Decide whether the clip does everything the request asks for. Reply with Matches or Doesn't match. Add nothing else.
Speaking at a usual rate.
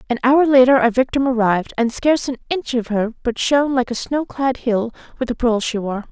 Doesn't match